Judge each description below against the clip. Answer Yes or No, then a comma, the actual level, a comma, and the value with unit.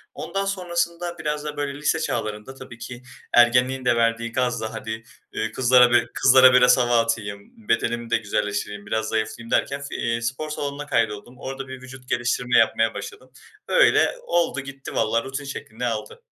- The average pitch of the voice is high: No, low, 125 Hz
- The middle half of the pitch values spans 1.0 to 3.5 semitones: Yes, average, 3.0 semitones